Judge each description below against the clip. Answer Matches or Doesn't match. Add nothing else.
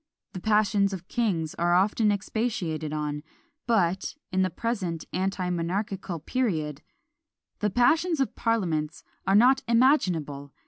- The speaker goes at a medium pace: Doesn't match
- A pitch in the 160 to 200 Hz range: Matches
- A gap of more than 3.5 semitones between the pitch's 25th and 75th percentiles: Matches